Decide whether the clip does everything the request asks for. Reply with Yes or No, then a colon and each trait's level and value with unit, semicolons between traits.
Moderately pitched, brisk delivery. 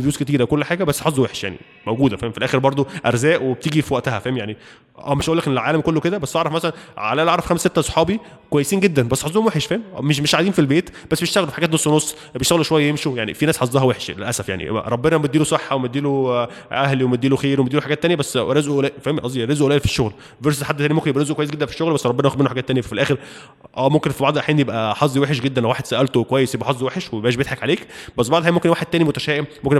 Yes: medium, 145 Hz; fast, 245 wpm